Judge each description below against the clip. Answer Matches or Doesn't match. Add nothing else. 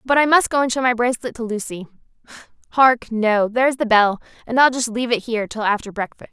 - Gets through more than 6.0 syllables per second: Matches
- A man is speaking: Doesn't match